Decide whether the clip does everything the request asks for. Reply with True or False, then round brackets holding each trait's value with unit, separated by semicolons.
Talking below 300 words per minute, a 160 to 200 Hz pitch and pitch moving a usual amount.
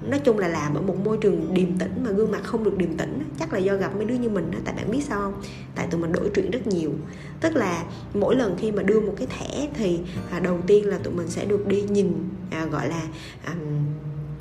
True (245 wpm; 185 Hz; 3.6 semitones)